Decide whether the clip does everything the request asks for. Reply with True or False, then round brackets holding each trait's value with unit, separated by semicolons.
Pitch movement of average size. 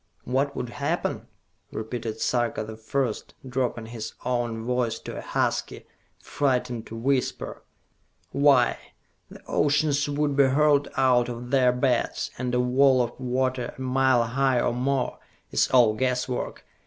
False (2.1 semitones)